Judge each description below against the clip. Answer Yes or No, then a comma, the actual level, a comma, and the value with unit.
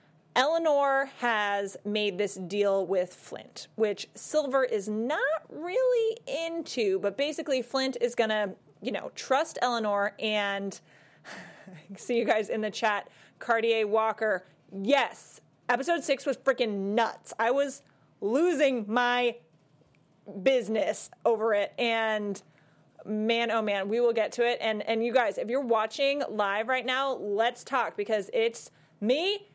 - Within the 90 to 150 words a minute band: Yes, average, 140 wpm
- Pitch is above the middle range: Yes, high, 225 Hz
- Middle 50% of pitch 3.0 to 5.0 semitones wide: Yes, average, 4.5 semitones